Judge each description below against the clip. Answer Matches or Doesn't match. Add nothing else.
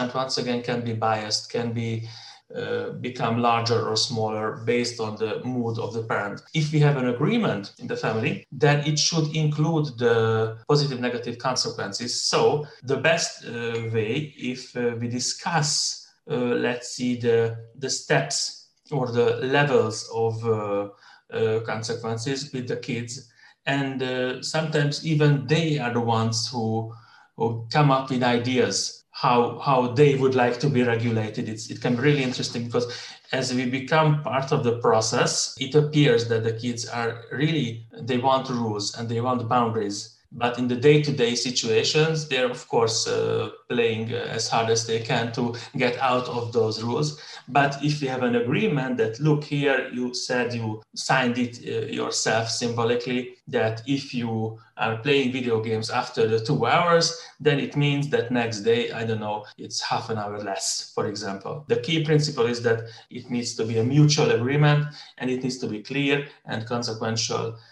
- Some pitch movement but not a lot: Matches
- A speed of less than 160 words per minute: Doesn't match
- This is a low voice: Matches